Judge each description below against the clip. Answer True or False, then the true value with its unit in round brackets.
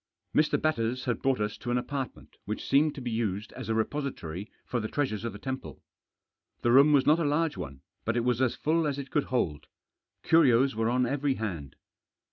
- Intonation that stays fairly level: False (4.2 semitones)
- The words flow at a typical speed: False (210 wpm)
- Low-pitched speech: True (125 Hz)